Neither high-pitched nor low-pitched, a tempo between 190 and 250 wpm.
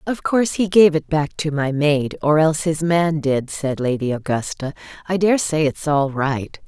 Yes: medium, 155 Hz; average, 200 wpm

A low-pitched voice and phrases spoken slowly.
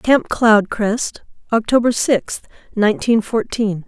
No: high, 220 Hz; slow, 95 wpm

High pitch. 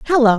Yes: very high, 250 Hz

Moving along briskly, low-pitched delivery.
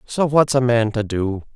Yes: fast, 230 wpm; low, 120 Hz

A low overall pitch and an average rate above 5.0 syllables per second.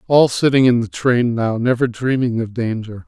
No: low, 120 Hz; 4.8 syllables/s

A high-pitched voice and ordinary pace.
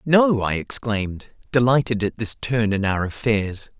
No: low, 115 Hz; average, 160 wpm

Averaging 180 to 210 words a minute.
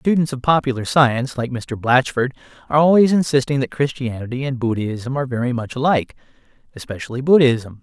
No: average, 155 wpm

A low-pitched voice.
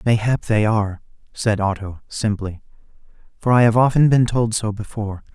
Yes: low, 110 Hz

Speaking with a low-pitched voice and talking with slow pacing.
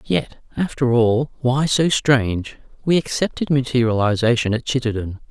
Yes: low, 125 Hz; slow, 125 wpm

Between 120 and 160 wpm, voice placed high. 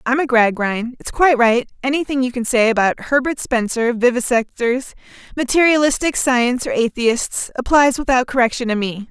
Yes: average, 140 wpm; very high, 250 Hz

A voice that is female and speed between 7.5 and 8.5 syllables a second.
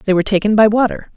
Yes: female; 7.9 syllables/s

